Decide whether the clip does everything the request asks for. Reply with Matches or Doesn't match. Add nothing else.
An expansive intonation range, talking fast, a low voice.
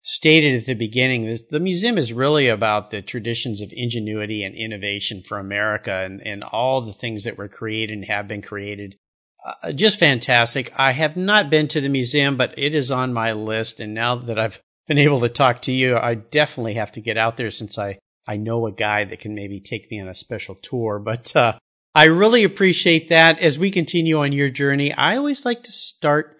Matches